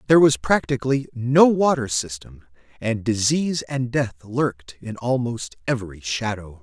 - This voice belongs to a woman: No, male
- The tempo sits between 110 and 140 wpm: Yes, slow, 135 wpm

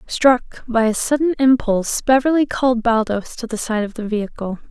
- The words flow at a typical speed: Yes, average, 180 wpm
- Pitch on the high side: Yes, high, 235 Hz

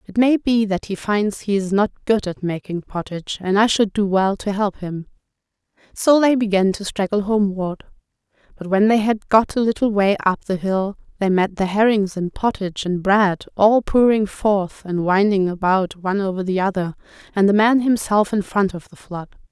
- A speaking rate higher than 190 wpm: Yes, average, 200 wpm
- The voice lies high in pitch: Yes, high, 200 Hz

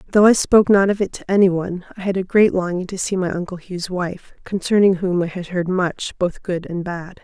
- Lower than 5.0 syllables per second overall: No, 5.4 syllables/s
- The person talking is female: Yes, female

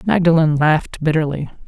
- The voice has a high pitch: No, medium, 160 Hz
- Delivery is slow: Yes, slow, 105 wpm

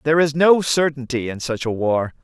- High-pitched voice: No, medium, 140 Hz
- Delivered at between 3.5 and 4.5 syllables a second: No, 5.4 syllables/s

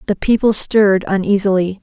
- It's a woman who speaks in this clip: Yes, female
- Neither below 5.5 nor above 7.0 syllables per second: Yes, 5.6 syllables/s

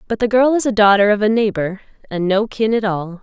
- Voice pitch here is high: Yes, high, 210 Hz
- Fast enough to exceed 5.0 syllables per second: Yes, 5.8 syllables/s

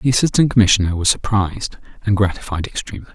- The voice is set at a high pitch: No, low, 105 Hz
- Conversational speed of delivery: Yes, average, 155 wpm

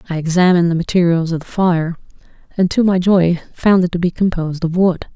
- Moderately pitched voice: Yes, medium, 175 Hz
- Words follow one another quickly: Yes, fast, 210 wpm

